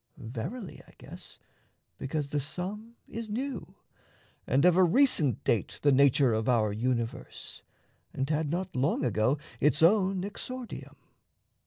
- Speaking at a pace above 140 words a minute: No, slow, 135 wpm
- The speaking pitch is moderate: Yes, medium, 150 Hz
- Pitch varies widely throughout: Yes, wide, 7.3 semitones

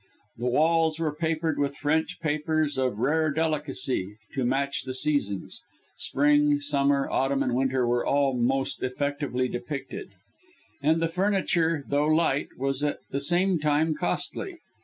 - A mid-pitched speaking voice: Yes, medium, 145 Hz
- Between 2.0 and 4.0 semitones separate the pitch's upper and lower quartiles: Yes, average, 2.8 semitones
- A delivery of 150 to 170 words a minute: No, average, 140 wpm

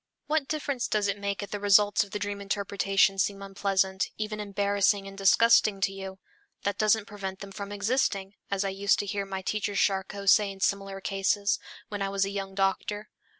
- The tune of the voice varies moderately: No, narrow, 0.9 semitones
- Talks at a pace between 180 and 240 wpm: Yes, average, 195 wpm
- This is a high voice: Yes, high, 200 Hz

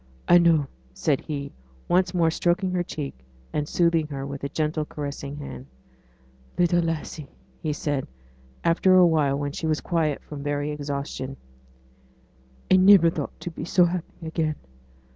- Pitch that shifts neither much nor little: Yes, average, 3.2 semitones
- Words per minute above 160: No, average, 150 wpm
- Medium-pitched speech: Yes, medium, 155 Hz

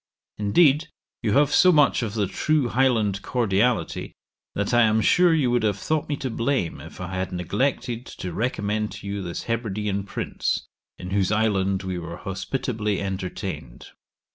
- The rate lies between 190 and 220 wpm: No, average, 165 wpm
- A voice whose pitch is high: No, low, 105 Hz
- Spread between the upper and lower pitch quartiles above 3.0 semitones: Yes, average, 4.5 semitones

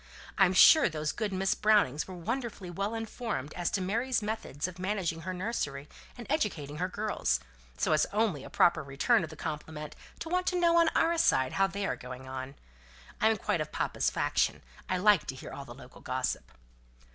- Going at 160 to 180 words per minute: No, average, 195 wpm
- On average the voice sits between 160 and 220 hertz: Yes, medium, 185 Hz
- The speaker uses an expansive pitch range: Yes, wide, 6.4 semitones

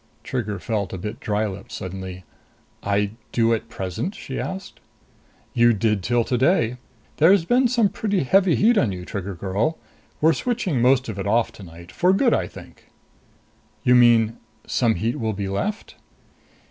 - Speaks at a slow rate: No, average, 160 wpm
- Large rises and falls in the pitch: Yes, wide, 8.5 semitones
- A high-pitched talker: No, low, 115 Hz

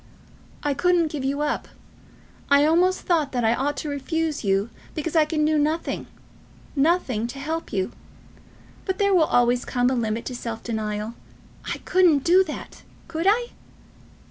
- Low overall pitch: No, very high, 295 Hz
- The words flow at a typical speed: Yes, average, 165 wpm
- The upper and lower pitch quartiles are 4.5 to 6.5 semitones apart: Yes, average, 5.2 semitones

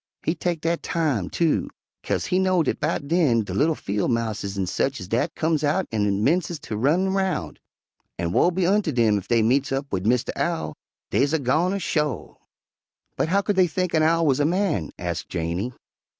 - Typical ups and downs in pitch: No, wide, 7.6 semitones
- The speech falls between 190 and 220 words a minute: Yes, average, 200 wpm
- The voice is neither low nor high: Yes, medium, 150 Hz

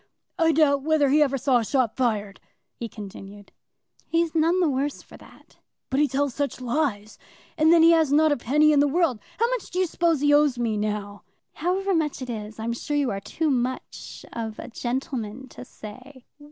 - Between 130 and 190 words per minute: No, fast, 205 wpm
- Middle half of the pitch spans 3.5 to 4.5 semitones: No, average, 5.0 semitones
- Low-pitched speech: No, very high, 275 Hz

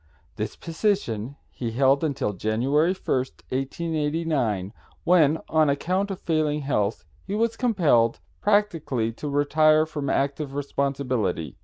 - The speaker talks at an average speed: No, slow, 120 wpm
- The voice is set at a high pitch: No, medium, 145 Hz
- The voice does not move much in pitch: No, average, 4.3 semitones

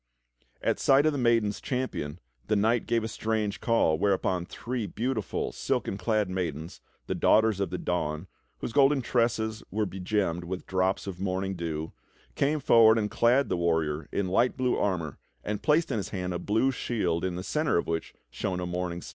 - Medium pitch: No, low, 100 Hz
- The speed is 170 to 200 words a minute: Yes, average, 190 wpm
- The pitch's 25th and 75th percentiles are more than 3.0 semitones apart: Yes, average, 4.6 semitones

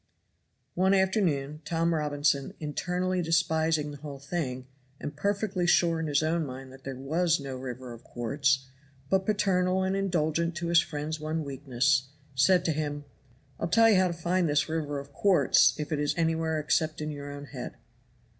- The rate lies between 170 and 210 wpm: Yes, average, 175 wpm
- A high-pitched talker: No, medium, 155 Hz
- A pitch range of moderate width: Yes, average, 3.4 semitones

